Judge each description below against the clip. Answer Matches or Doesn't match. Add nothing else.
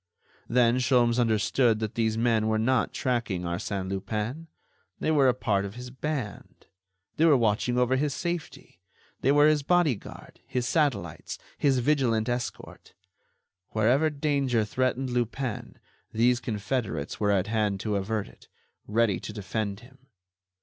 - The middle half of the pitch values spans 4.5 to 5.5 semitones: Doesn't match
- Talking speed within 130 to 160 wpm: Matches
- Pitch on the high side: Doesn't match